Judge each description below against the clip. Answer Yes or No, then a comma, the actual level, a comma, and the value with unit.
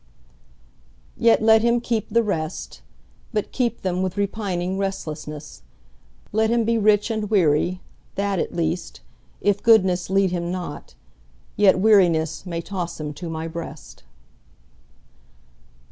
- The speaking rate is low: Yes, slow, 115 wpm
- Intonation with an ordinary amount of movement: Yes, average, 4.3 semitones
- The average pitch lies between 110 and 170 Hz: No, medium, 185 Hz